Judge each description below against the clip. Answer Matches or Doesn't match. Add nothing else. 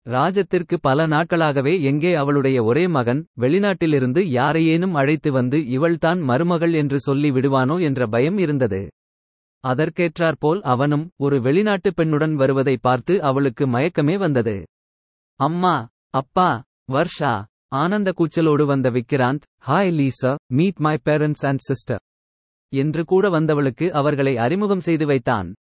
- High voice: Doesn't match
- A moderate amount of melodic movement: Matches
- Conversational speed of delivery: Matches